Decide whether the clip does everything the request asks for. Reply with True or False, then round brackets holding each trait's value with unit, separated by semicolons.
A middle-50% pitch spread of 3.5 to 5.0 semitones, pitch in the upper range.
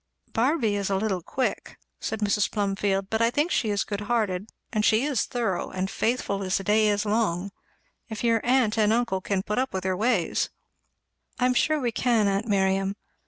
False (3.1 semitones; 210 Hz)